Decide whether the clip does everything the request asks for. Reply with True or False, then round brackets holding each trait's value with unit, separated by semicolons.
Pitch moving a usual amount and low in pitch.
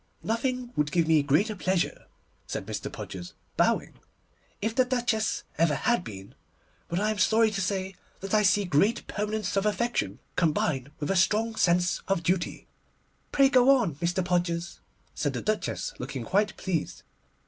False (4.8 semitones; 190 Hz)